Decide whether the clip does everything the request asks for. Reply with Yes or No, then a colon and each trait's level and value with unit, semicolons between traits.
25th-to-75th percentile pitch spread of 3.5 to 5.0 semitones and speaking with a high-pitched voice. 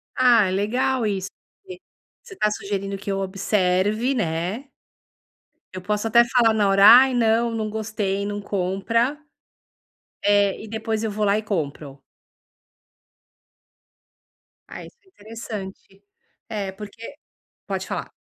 No: average, 2.7 semitones; high, 210 Hz